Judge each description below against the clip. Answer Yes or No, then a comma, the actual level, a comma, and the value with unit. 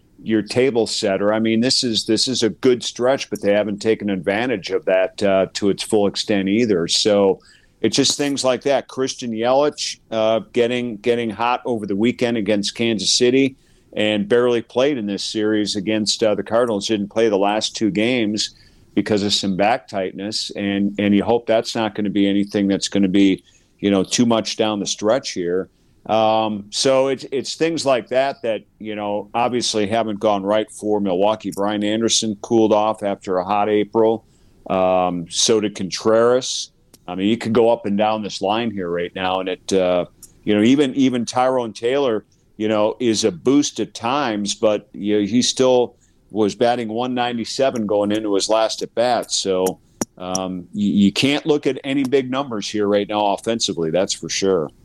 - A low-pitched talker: Yes, low, 110 Hz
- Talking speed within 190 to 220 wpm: Yes, average, 195 wpm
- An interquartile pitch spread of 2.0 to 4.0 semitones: Yes, average, 2.9 semitones